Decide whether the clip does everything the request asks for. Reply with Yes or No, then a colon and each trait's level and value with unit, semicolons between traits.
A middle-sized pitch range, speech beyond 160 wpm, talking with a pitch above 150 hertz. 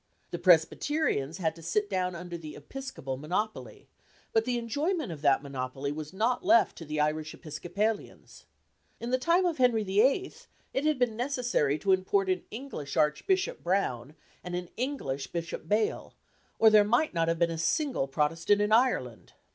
No: wide, 7.9 semitones; average, 170 wpm; high, 190 Hz